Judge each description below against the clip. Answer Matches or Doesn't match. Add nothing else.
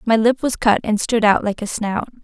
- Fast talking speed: Matches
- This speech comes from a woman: Matches